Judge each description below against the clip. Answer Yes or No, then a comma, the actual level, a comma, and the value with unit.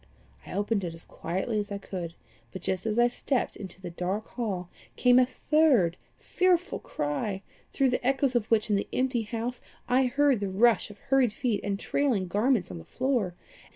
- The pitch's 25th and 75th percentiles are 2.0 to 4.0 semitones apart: No, average, 4.9 semitones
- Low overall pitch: No, high, 220 Hz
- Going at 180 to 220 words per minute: Yes, average, 190 wpm